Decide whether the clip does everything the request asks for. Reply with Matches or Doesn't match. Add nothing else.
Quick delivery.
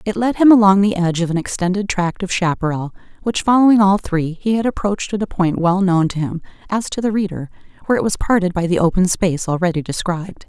Matches